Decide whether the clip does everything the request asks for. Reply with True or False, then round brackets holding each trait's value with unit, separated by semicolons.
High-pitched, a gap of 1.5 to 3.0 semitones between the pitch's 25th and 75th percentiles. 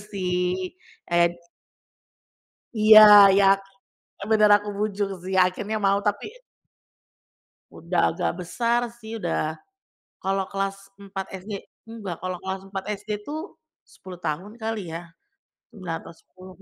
True (195 Hz; 2.6 semitones)